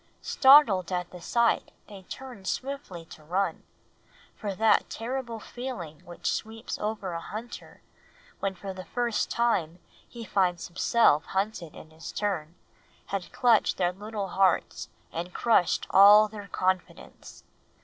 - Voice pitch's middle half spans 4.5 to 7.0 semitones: No, average, 4.1 semitones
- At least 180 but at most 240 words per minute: No, slow, 135 wpm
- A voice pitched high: Yes, high, 200 Hz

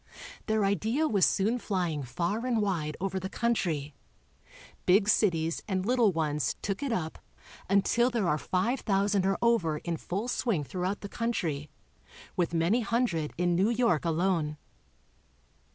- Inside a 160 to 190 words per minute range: No, average, 150 wpm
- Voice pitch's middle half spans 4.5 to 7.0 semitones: Yes, average, 5.2 semitones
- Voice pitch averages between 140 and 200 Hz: Yes, high, 190 Hz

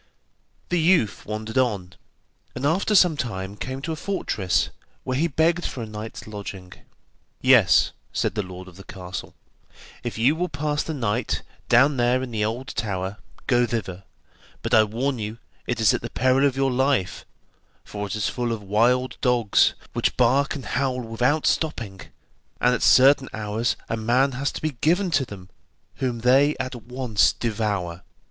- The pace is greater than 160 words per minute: Yes, average, 175 wpm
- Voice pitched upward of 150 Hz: No, low, 120 Hz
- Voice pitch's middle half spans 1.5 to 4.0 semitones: No, average, 4.4 semitones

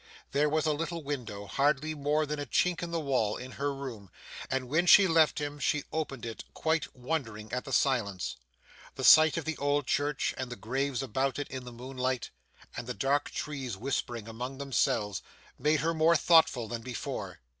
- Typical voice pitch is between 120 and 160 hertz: Yes, medium, 140 Hz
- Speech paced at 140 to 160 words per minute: No, average, 190 wpm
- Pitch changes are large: No, average, 3.6 semitones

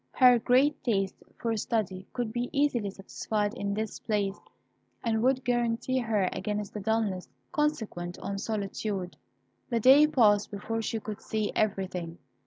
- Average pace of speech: Yes, average, 145 wpm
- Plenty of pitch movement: No, average, 3.2 semitones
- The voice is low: No, high, 220 Hz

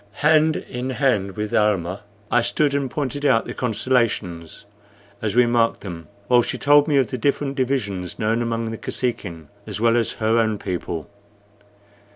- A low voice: Yes, low, 115 Hz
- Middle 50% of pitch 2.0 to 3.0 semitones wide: No, average, 4.2 semitones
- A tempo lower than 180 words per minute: Yes, average, 170 wpm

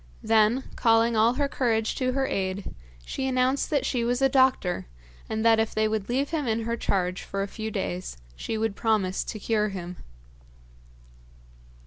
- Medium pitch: No, high, 225 Hz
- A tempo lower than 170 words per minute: No, average, 175 wpm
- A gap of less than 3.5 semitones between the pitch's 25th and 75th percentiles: No, average, 3.8 semitones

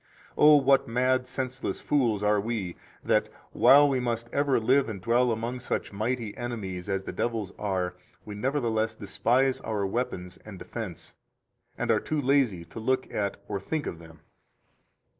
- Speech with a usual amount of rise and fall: Yes, average, 4.3 semitones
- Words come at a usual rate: Yes, average, 165 wpm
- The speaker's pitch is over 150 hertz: No, low, 115 Hz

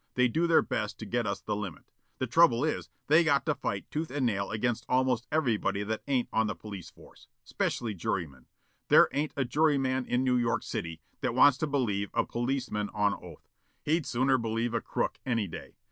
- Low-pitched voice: Yes, low, 120 Hz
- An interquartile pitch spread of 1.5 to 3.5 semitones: No, average, 4.7 semitones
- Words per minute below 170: No, average, 200 wpm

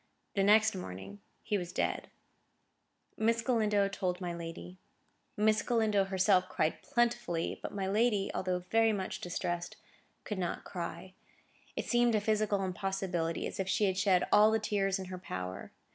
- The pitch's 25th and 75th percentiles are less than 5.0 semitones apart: Yes, average, 3.1 semitones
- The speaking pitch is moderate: No, high, 195 Hz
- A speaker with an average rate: Yes, average, 160 wpm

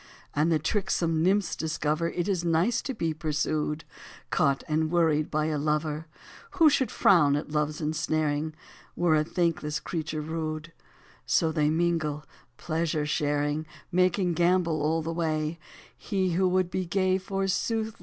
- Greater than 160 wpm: No, average, 150 wpm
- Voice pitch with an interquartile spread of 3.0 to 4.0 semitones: No, narrow, 2.5 semitones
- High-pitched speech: No, medium, 160 Hz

